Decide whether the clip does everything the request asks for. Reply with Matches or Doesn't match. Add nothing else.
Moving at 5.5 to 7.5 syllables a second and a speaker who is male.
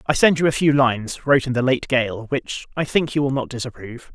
Matches